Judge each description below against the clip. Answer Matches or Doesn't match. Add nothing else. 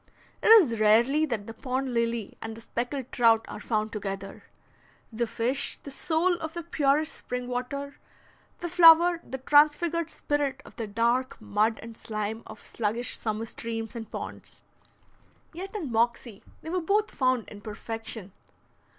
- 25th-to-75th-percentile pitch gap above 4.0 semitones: Matches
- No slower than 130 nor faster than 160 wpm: Matches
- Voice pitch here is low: Doesn't match